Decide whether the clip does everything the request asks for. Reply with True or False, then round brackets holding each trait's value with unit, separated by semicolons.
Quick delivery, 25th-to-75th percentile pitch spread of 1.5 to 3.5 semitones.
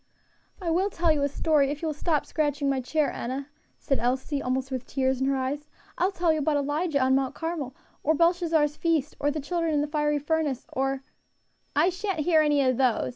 True (225 wpm; 3.0 semitones)